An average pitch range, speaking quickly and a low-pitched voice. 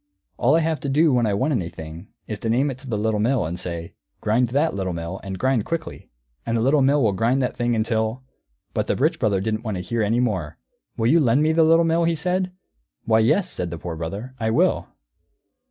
No: wide, 5.9 semitones; fast, 240 wpm; low, 115 Hz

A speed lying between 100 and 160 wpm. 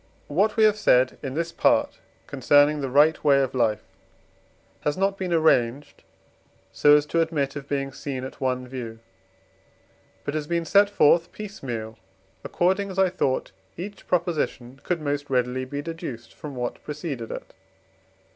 Yes: average, 155 wpm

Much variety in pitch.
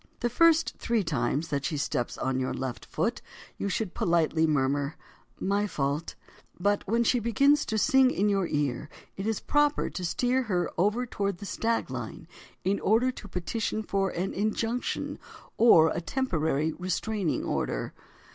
Yes: wide, 6.4 semitones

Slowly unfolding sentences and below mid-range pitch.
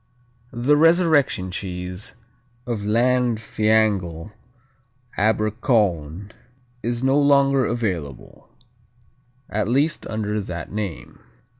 Yes: slow, 80 wpm; low, 110 Hz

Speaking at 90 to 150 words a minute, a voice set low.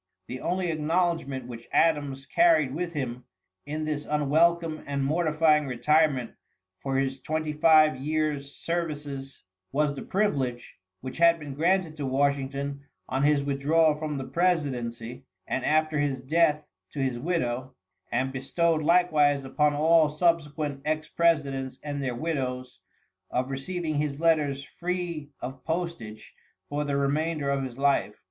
No: average, 140 wpm; medium, 145 Hz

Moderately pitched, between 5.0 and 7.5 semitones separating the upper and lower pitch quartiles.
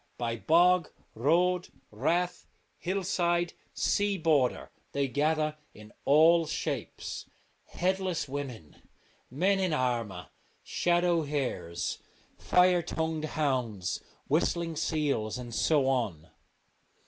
Yes: medium, 155 Hz; wide, 5.6 semitones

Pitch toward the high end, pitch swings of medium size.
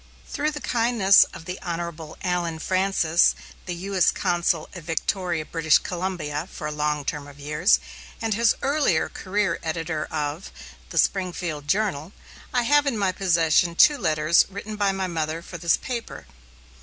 No: medium, 175 Hz; average, 3.8 semitones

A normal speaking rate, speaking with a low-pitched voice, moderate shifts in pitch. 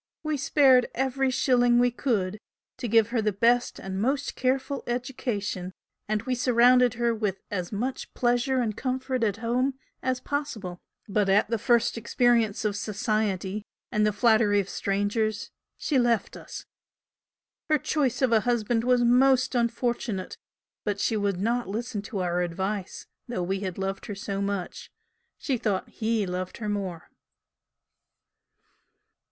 No: average, 150 wpm; high, 230 Hz; average, 3.6 semitones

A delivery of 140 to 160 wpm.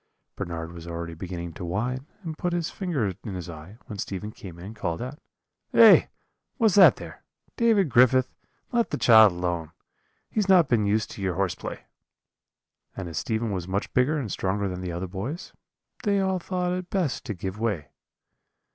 No: average, 185 wpm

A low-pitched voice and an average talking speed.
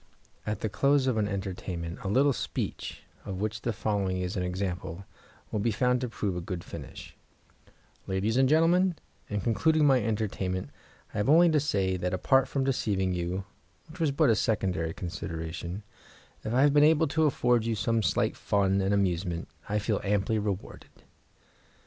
Yes: low, 105 Hz; average, 175 wpm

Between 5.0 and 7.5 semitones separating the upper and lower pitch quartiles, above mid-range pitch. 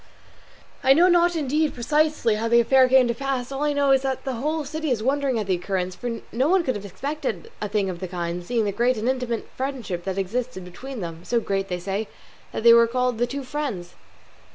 Yes: wide, 5.4 semitones; high, 245 Hz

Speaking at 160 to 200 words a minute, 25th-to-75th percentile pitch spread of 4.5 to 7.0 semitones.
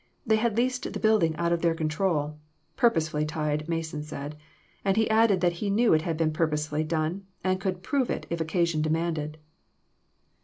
No: average, 185 wpm; average, 4.0 semitones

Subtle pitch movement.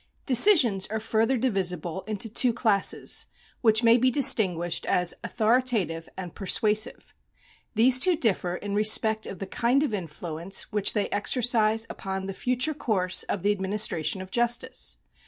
No: average, 4.0 semitones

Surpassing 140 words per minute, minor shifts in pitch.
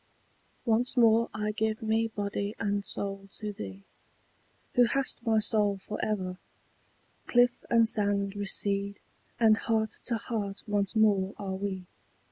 No: slow, 135 wpm; narrow, 2.0 semitones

